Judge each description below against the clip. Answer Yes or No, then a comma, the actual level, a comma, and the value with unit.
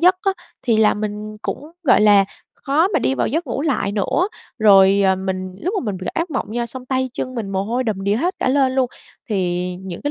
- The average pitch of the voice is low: No, high, 220 Hz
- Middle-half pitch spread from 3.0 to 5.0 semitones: No, wide, 5.6 semitones